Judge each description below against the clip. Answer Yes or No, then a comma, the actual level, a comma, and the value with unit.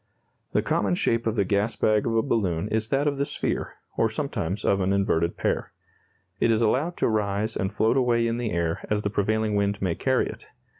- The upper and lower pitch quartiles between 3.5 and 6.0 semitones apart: No, average, 2.8 semitones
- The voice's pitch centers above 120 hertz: No, low, 105 Hz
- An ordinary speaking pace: No, fast, 215 wpm